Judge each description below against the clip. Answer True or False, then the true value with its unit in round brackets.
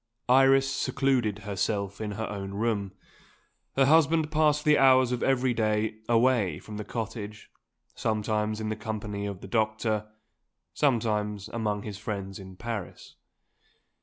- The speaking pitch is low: True (110 Hz)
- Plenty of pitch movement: False (3.3 semitones)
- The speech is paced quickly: False (135 wpm)